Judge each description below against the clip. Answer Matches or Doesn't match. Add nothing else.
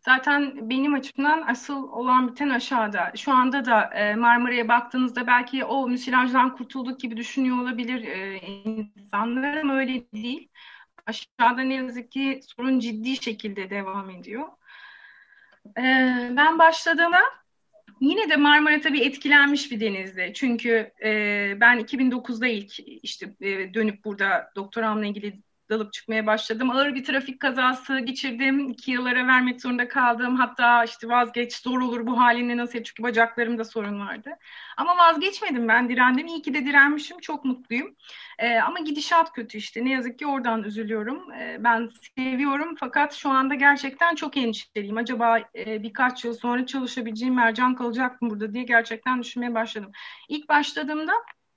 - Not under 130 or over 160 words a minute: Matches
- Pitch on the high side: Matches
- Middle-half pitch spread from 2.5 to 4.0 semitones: Matches